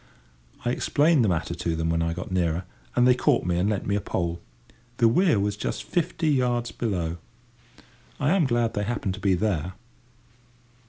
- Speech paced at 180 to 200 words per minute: Yes, average, 190 wpm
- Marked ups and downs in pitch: Yes, wide, 5.9 semitones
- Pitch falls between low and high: No, low, 105 Hz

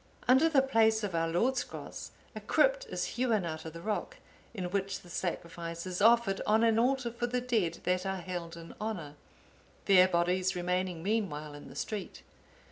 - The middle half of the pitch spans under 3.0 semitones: No, average, 4.9 semitones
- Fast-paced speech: No, average, 185 wpm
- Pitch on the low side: No, high, 190 Hz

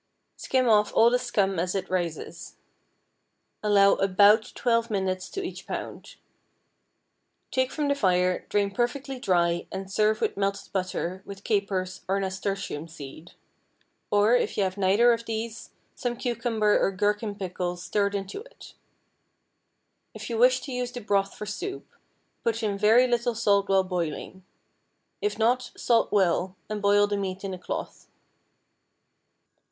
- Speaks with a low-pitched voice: No, high, 205 Hz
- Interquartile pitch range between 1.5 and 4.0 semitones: Yes, average, 3.6 semitones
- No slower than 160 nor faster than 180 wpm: No, average, 150 wpm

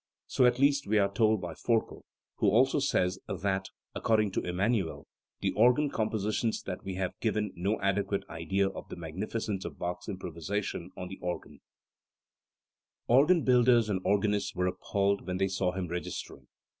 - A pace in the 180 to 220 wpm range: No, average, 160 wpm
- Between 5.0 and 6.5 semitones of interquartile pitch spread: No, average, 3.4 semitones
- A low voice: Yes, low, 100 Hz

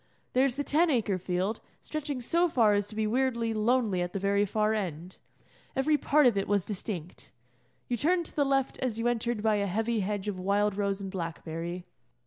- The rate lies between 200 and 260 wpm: Yes, fast, 205 wpm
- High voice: Yes, high, 215 Hz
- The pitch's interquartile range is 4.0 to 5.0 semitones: Yes, average, 4.5 semitones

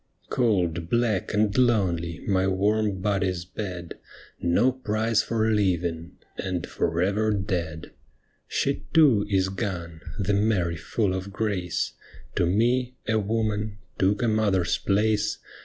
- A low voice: Yes, low, 100 Hz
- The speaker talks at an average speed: No, slow, 130 wpm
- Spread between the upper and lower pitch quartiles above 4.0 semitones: No, average, 3.2 semitones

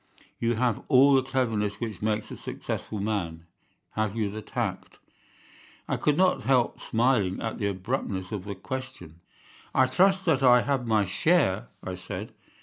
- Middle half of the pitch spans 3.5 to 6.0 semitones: Yes, average, 4.6 semitones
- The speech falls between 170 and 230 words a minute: No, average, 160 wpm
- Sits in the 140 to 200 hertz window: No, low, 110 Hz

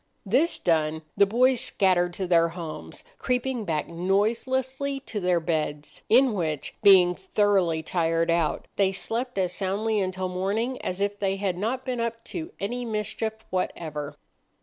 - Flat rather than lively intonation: No, average, 4.9 semitones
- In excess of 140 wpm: Yes, average, 150 wpm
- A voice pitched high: Yes, high, 195 Hz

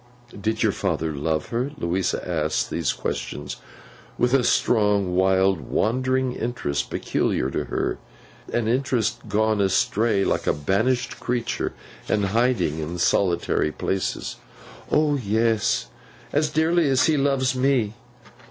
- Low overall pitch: Yes, low, 110 Hz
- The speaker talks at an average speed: No, slow, 125 wpm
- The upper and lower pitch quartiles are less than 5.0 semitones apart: No, average, 5.3 semitones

